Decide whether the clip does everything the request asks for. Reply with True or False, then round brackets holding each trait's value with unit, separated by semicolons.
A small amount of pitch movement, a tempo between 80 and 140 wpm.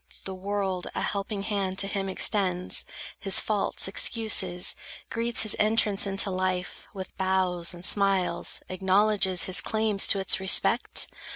True (1.7 semitones; 135 wpm)